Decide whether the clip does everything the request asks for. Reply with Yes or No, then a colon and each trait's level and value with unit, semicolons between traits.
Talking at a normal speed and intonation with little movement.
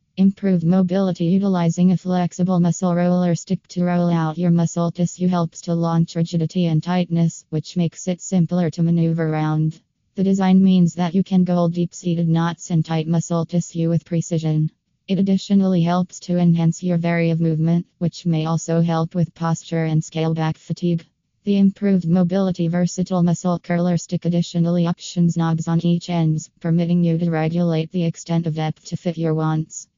Yes: average, 170 wpm; narrow, 1.3 semitones